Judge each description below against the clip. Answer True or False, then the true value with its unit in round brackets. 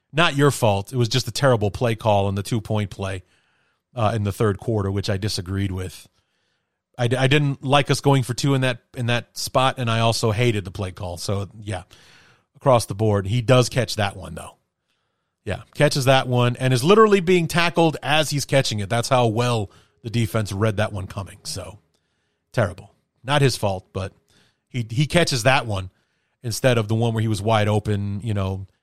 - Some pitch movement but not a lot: True (4.4 semitones)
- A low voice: True (115 Hz)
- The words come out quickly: True (210 wpm)